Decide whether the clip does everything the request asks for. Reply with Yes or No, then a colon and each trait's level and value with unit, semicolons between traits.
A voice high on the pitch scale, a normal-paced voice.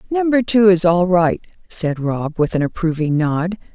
No: medium, 180 Hz; average, 175 wpm